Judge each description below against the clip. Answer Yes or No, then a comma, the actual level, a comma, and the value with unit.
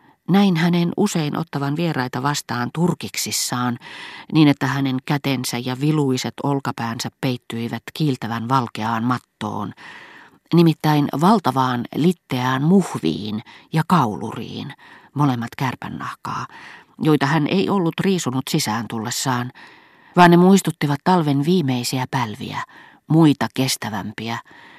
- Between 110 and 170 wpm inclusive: No, average, 100 wpm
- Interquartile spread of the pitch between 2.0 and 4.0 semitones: No, average, 4.9 semitones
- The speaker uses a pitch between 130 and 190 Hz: Yes, low, 135 Hz